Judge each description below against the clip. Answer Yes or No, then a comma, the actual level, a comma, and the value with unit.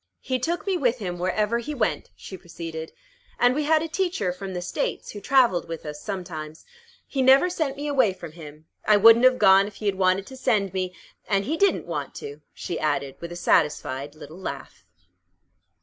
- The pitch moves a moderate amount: No, wide, 7.2 semitones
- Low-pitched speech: No, high, 195 Hz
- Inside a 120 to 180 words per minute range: No, average, 200 wpm